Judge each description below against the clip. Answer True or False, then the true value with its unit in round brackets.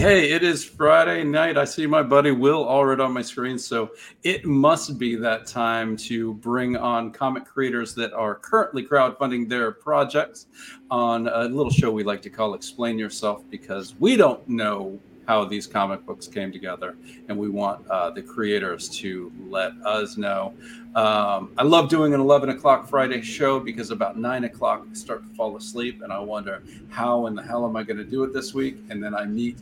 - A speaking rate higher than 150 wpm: True (200 wpm)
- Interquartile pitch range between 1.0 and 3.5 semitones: False (4.2 semitones)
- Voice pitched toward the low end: True (120 Hz)